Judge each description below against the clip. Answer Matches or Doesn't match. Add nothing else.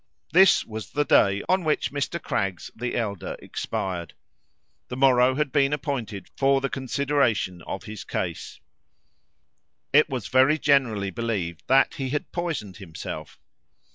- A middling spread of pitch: Doesn't match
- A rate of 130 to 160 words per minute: Matches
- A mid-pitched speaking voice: Doesn't match